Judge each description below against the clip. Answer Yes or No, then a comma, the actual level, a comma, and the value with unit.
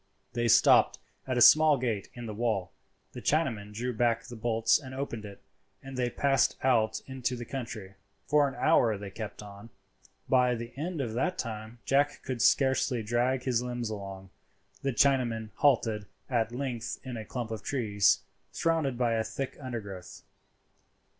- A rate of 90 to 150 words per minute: No, average, 165 wpm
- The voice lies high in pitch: No, low, 120 Hz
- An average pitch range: Yes, average, 3.2 semitones